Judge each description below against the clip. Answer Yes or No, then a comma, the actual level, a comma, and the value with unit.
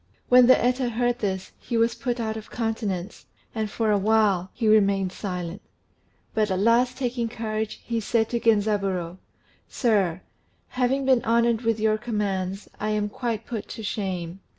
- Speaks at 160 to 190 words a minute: Yes, average, 170 wpm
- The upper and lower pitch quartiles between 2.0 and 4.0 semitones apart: Yes, average, 3.0 semitones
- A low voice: No, high, 220 Hz